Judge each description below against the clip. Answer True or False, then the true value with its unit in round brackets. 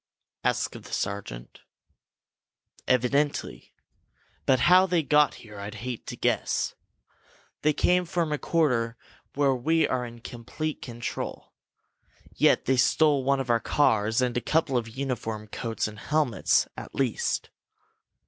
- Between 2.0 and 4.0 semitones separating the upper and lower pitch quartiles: False (4.5 semitones)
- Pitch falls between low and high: False (125 Hz)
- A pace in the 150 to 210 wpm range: False (135 wpm)